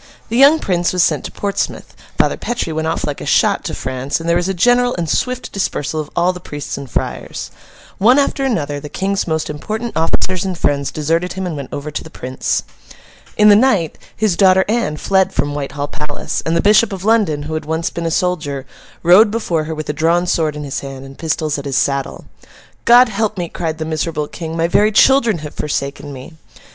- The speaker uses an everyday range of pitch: Yes, average, 5.0 semitones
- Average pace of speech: No, fast, 220 wpm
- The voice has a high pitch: No, medium, 165 Hz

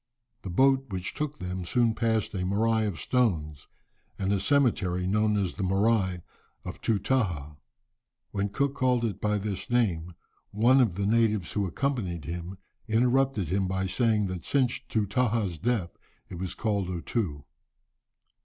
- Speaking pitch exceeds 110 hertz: No, low, 100 Hz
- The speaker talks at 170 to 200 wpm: No, average, 155 wpm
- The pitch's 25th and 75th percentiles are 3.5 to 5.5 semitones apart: Yes, average, 4.2 semitones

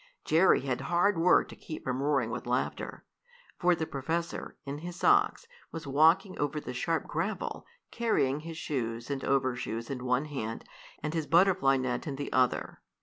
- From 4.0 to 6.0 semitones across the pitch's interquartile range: Yes, average, 4.4 semitones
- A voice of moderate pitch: Yes, medium, 145 Hz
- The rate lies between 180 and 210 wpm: No, average, 170 wpm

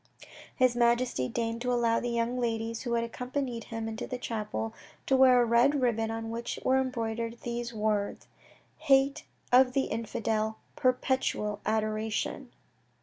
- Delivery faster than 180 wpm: No, average, 145 wpm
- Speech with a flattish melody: Yes, narrow, 2.1 semitones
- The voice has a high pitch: Yes, high, 235 Hz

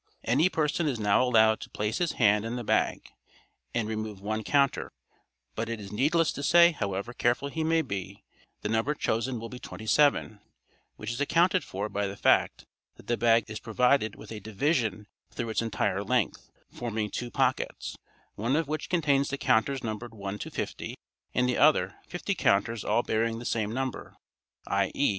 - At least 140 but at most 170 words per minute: No, average, 180 wpm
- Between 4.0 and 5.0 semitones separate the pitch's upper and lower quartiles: Yes, average, 4.5 semitones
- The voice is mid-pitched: No, low, 115 Hz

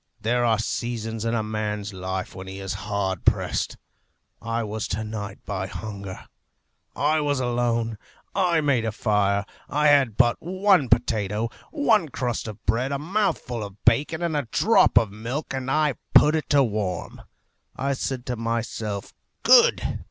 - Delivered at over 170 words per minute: No, average, 160 wpm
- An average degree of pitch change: Yes, average, 5.0 semitones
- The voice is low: Yes, low, 115 Hz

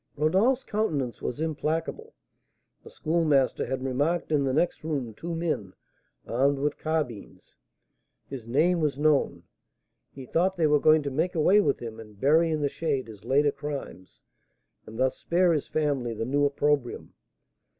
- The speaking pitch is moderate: Yes, medium, 145 Hz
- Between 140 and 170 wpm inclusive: Yes, average, 160 wpm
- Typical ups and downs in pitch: Yes, average, 3.6 semitones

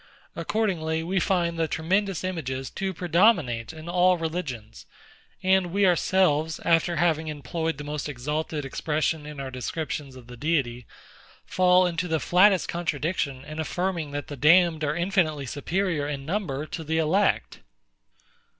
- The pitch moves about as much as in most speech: Yes, average, 3.5 semitones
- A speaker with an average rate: Yes, average, 145 wpm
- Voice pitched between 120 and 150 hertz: No, medium, 160 Hz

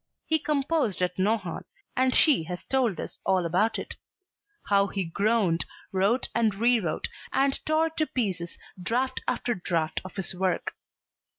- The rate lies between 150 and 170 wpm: Yes, average, 155 wpm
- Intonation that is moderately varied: No, wide, 6.1 semitones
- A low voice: No, high, 205 Hz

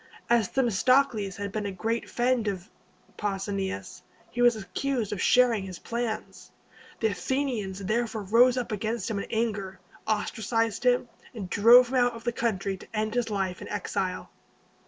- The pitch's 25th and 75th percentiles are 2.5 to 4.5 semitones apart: Yes, average, 3.3 semitones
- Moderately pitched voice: No, high, 220 Hz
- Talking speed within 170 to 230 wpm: No, average, 160 wpm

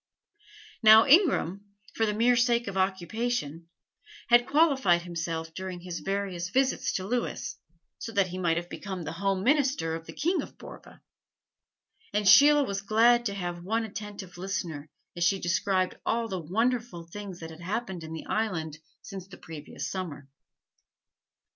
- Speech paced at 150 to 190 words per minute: Yes, average, 160 wpm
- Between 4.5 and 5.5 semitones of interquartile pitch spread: Yes, average, 4.8 semitones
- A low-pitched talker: No, high, 195 Hz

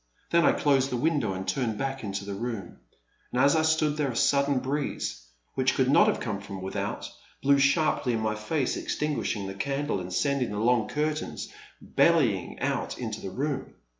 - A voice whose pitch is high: No, low, 130 Hz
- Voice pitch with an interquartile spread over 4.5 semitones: Yes, average, 5.3 semitones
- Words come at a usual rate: Yes, average, 190 wpm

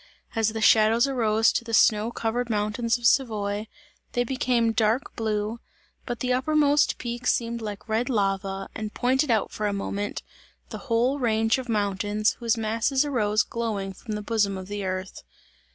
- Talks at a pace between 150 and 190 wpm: Yes, average, 170 wpm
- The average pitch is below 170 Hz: No, high, 225 Hz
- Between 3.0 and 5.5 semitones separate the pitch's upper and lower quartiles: No, narrow, 2.4 semitones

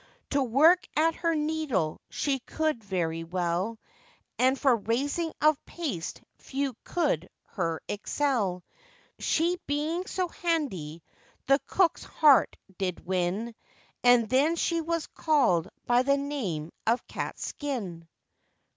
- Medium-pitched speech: No, very high, 265 Hz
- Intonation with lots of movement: Yes, wide, 8.7 semitones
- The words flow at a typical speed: No, slow, 120 wpm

